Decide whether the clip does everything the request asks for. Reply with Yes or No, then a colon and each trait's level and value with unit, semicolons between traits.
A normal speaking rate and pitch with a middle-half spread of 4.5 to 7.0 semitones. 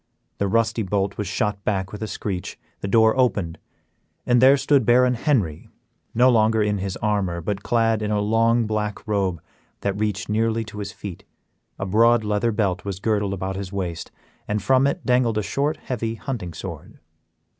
No: average, 180 wpm; average, 2.7 semitones